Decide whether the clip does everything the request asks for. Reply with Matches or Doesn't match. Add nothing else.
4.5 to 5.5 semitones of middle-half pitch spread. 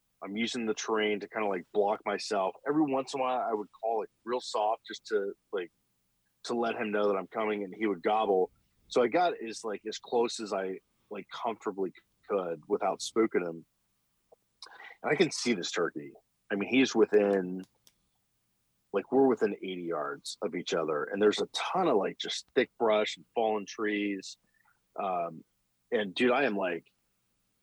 Matches